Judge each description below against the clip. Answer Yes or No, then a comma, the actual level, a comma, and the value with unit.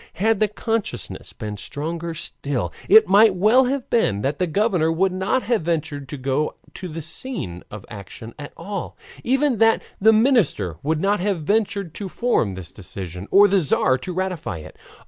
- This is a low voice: No, medium, 175 Hz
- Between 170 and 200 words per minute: Yes, average, 180 wpm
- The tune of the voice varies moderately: No, wide, 7.5 semitones